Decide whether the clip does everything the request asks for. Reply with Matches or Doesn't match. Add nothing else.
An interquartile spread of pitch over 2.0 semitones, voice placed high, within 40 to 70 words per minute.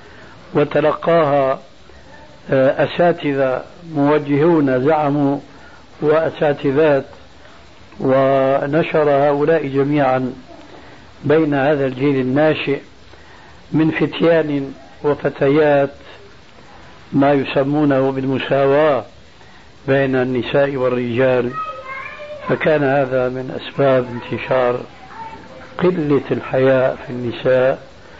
Doesn't match